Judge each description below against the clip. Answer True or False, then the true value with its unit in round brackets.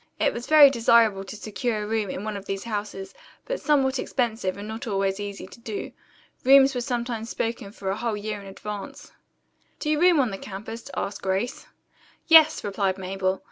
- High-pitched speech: True (215 Hz)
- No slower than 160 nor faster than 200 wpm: True (190 wpm)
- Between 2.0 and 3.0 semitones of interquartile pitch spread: False (3.7 semitones)